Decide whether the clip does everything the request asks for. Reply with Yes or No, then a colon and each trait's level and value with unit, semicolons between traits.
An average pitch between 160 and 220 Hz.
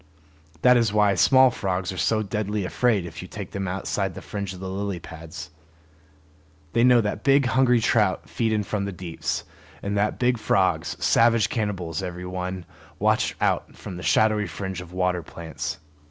No: low, 100 Hz